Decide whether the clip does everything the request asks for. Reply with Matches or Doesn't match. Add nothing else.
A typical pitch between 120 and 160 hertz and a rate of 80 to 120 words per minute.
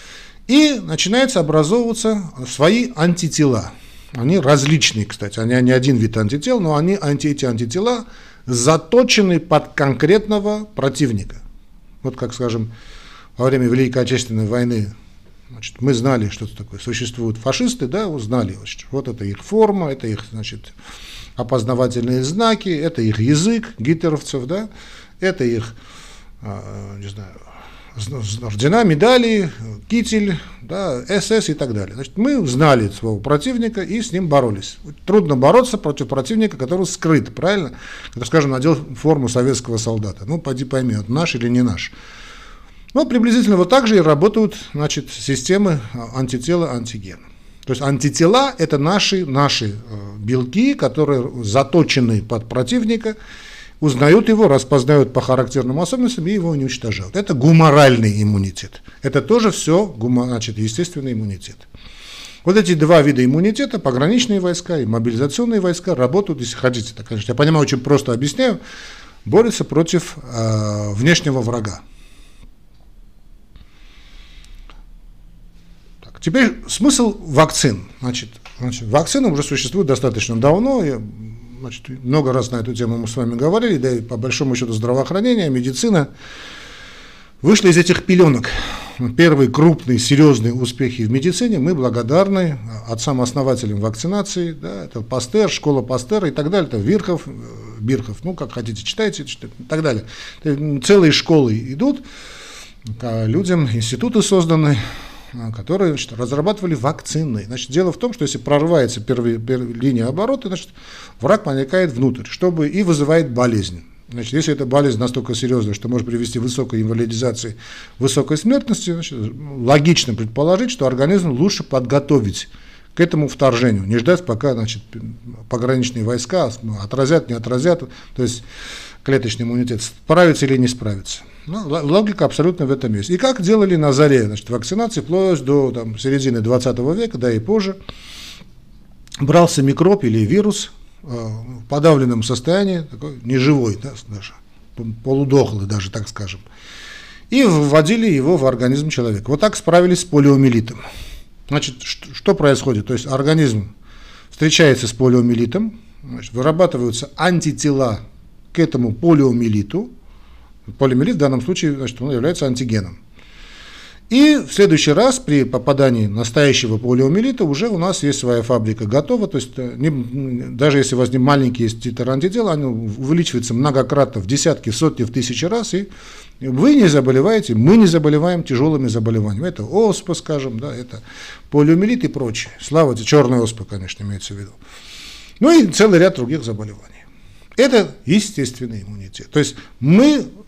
Doesn't match